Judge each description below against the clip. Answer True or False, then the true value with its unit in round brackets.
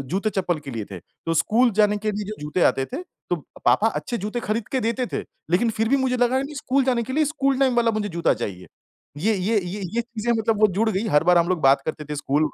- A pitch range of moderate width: False (5.8 semitones)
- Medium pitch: False (215 Hz)